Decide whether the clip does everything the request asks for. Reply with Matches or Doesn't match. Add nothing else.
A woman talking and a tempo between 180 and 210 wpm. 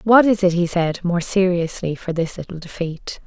Matches